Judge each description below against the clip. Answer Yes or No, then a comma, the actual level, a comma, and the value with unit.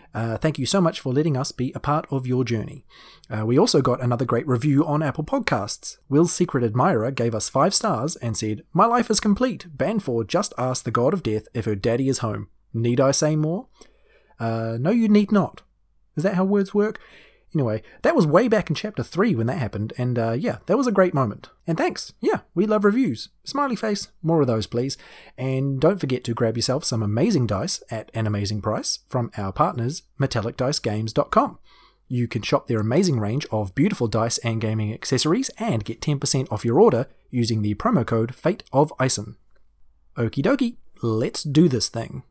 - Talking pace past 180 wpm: Yes, average, 200 wpm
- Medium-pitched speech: No, low, 130 Hz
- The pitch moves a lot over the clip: Yes, wide, 6.2 semitones